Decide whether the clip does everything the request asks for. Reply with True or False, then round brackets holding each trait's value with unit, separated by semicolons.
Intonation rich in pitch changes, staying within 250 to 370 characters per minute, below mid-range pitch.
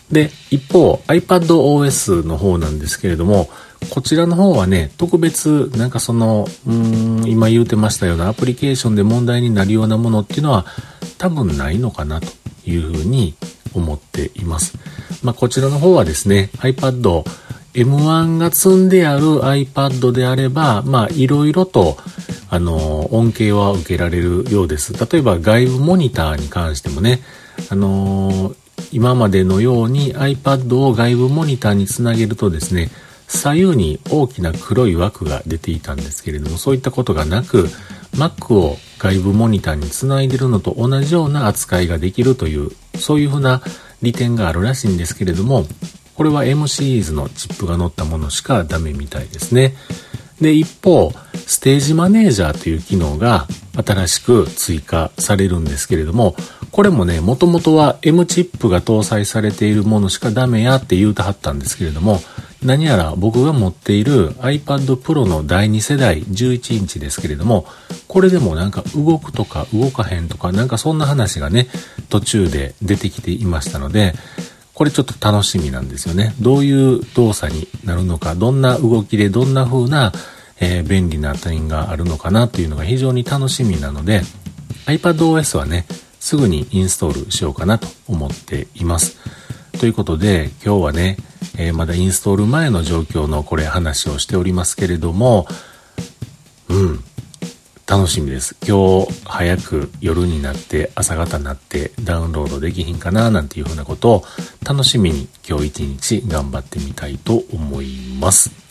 True (7.0 semitones; 355 characters per minute; 110 Hz)